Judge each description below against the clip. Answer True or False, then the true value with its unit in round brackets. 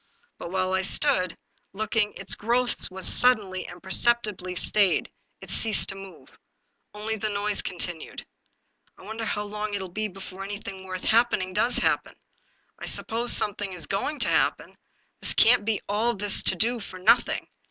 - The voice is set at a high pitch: True (205 Hz)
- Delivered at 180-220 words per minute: False (170 wpm)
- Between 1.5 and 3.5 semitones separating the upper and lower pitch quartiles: True (2.8 semitones)